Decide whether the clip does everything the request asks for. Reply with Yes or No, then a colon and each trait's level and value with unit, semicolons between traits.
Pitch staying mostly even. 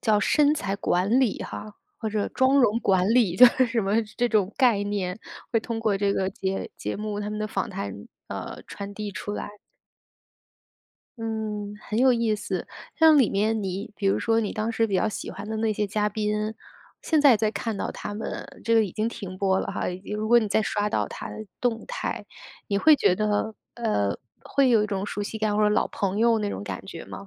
Yes: narrow, 2.0 semitones